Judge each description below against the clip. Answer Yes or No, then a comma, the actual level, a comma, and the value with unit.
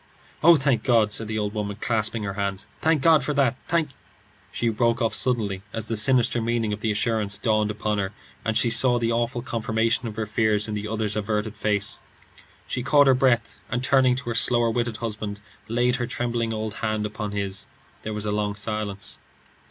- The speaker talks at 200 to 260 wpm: Yes, fast, 205 wpm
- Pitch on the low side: Yes, low, 110 Hz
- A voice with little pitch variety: Yes, narrow, 2.2 semitones